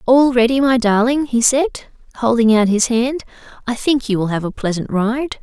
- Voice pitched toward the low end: No, high, 240 Hz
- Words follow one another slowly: No, average, 200 wpm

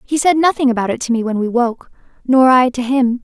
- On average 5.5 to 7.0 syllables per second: Yes, 5.9 syllables/s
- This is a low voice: No, very high, 250 Hz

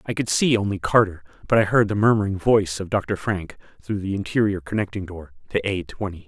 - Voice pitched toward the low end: Yes, low, 100 Hz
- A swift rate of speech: Yes, fast, 210 wpm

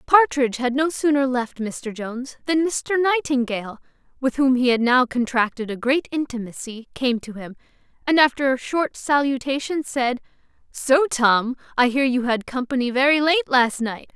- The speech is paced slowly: No, average, 165 wpm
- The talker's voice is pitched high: Yes, very high, 260 Hz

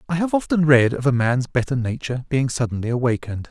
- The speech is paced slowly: No, fast, 205 wpm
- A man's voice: Yes, male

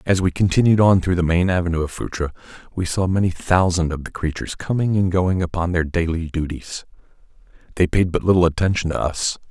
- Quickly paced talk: No, average, 195 wpm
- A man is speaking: Yes, male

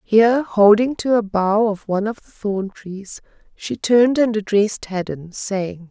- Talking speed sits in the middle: Yes, average, 175 wpm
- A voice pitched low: No, high, 210 Hz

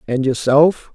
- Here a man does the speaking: Yes, male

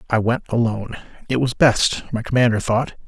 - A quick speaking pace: No, average, 175 wpm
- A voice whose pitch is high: No, low, 120 Hz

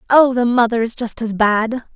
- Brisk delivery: Yes, fast, 215 wpm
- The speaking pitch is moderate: No, high, 235 Hz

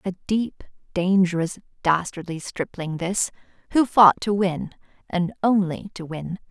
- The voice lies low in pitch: No, medium, 185 Hz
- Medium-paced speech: No, slow, 130 wpm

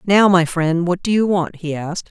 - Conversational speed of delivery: No, fast, 255 wpm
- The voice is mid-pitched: Yes, medium, 175 Hz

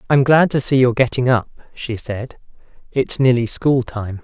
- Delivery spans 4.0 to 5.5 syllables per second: Yes, 4.9 syllables/s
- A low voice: Yes, low, 125 Hz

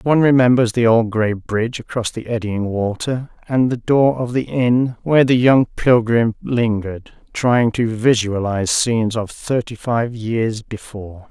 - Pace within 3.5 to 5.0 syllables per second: Yes, 4.5 syllables/s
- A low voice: Yes, low, 115 Hz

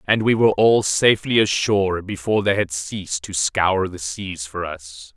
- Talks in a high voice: No, very low, 95 Hz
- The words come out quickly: No, average, 185 wpm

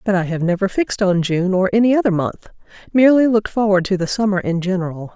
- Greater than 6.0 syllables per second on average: Yes, 6.5 syllables/s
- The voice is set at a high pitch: Yes, high, 195 Hz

